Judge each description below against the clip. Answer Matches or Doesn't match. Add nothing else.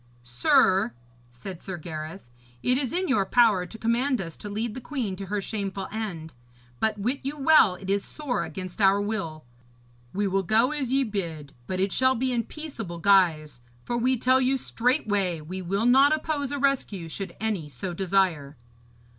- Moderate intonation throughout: Doesn't match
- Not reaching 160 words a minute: Doesn't match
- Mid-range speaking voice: Doesn't match